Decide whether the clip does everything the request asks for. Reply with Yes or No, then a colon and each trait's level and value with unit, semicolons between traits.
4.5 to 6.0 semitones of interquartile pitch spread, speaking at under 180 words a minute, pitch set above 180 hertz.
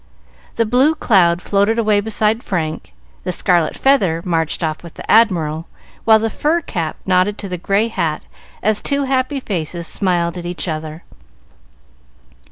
Yes: average, 4.9 semitones; average, 155 wpm; high, 190 Hz